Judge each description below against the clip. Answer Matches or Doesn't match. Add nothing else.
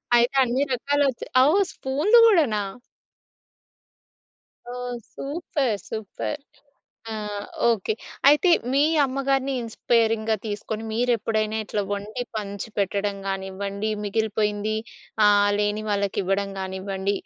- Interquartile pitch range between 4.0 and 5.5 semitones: Matches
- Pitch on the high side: Matches